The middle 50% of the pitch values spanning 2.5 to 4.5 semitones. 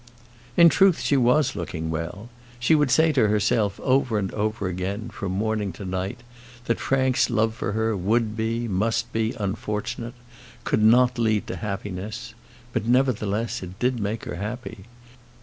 Yes: average, 3.2 semitones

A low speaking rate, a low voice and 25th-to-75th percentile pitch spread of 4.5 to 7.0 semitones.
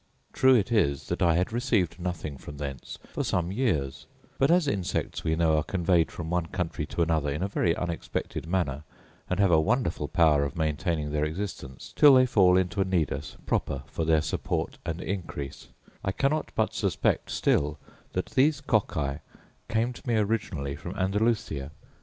No: average, 175 wpm; very low, 85 Hz; average, 5.1 semitones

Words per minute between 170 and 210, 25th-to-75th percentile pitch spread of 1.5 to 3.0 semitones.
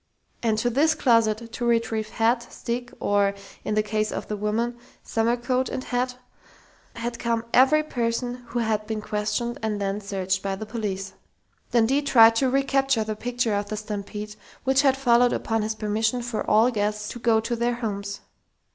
Yes: average, 180 wpm; narrow, 2.4 semitones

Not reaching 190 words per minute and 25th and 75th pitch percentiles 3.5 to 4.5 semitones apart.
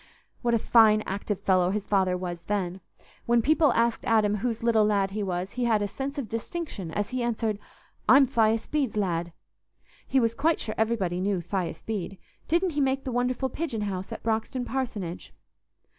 Yes: average, 180 wpm; average, 4.1 semitones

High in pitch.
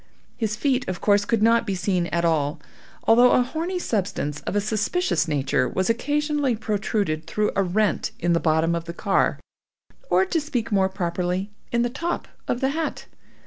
Yes: high, 210 Hz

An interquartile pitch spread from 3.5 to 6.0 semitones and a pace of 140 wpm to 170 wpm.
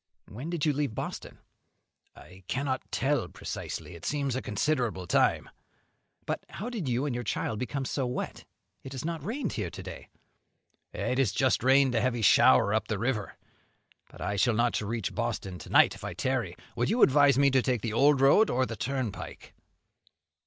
No: average, 4.0 semitones; average, 190 wpm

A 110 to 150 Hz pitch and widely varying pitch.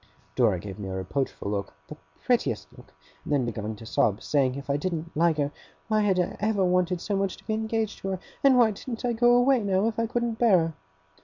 No: medium, 185 Hz; wide, 8.3 semitones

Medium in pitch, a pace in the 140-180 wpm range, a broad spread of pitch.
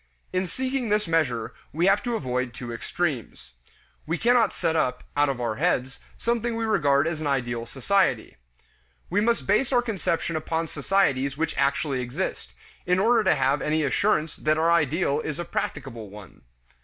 Yes: medium, 155 Hz; average, 170 wpm; wide, 7.0 semitones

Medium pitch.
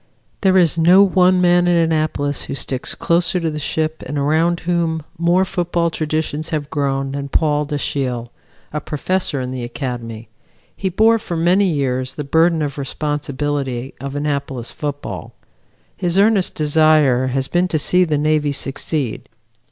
Yes: medium, 150 Hz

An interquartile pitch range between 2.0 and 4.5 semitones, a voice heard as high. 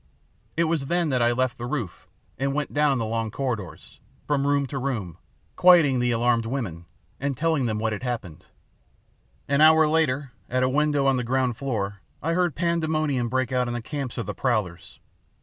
No: average, 4.0 semitones; low, 130 Hz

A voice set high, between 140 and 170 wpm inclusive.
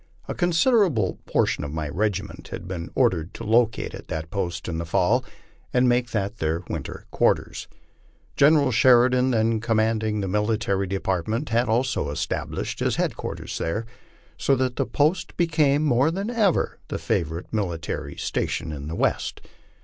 No: low, 110 Hz; average, 155 wpm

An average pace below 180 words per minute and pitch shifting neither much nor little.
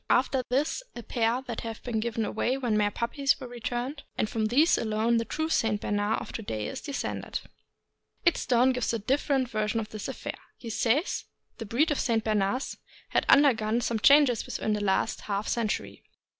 No: average, 185 wpm; average, 3.3 semitones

